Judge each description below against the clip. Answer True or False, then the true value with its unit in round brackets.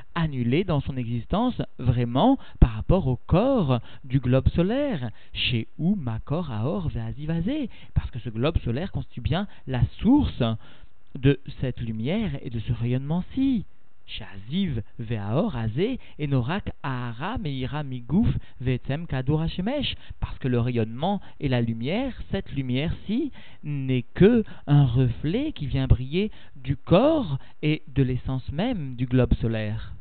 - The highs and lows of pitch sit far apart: True (6.6 semitones)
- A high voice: False (135 Hz)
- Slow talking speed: True (130 wpm)